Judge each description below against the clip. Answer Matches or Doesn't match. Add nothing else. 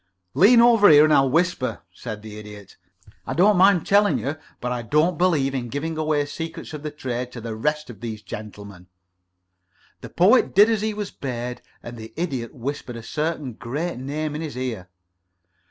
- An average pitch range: Doesn't match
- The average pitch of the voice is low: Doesn't match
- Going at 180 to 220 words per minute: Matches